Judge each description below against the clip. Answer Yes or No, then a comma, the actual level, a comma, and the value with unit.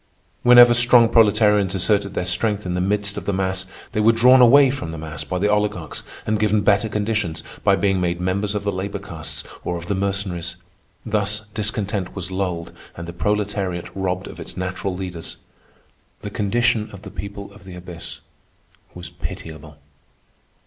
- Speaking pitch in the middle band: No, low, 100 Hz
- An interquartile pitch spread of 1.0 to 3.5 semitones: Yes, narrow, 2.6 semitones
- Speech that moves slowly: No, average, 175 wpm